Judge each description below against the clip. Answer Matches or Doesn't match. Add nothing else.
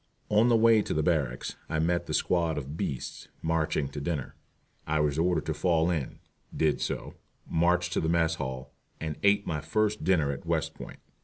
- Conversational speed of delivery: Matches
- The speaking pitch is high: Doesn't match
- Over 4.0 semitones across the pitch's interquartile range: Doesn't match